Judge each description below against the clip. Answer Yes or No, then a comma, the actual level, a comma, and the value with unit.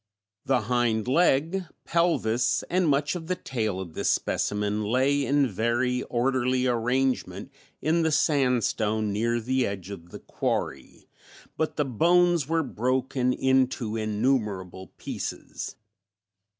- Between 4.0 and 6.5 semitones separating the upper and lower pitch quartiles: Yes, average, 4.5 semitones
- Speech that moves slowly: Yes, slow, 125 wpm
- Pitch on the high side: No, low, 125 Hz